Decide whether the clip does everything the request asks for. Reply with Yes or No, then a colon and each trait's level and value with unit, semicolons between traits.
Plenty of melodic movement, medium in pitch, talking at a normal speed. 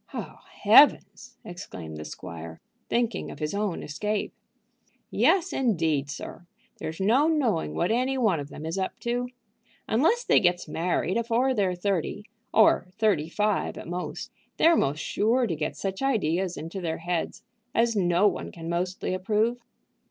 No: wide, 5.9 semitones; high, 195 Hz; average, 155 wpm